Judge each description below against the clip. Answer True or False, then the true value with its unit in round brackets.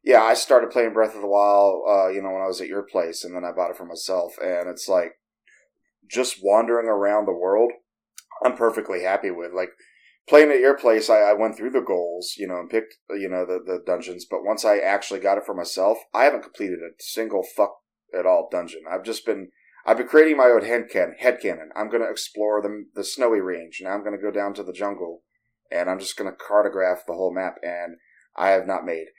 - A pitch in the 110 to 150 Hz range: False (100 Hz)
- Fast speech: True (230 wpm)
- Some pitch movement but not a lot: True (3.6 semitones)